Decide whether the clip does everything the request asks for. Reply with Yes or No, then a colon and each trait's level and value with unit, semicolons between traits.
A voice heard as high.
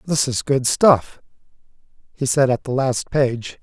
No: low, 130 Hz